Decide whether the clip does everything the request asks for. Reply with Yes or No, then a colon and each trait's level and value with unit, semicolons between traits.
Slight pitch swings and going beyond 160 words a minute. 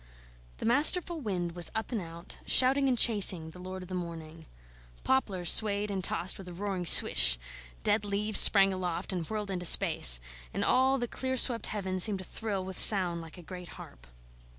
No: average, 3.8 semitones; average, 190 wpm